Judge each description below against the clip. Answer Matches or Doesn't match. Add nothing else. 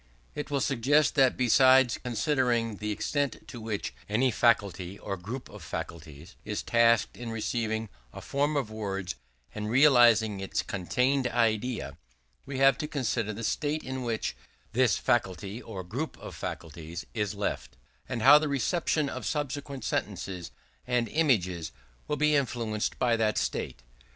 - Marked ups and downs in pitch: Doesn't match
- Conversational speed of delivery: Matches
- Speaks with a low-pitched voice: Matches